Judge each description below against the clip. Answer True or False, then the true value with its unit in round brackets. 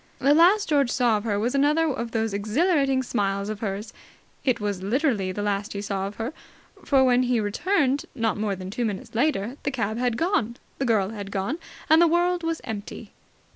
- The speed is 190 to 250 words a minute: True (205 wpm)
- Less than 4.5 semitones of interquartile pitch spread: False (5.5 semitones)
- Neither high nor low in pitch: False (235 Hz)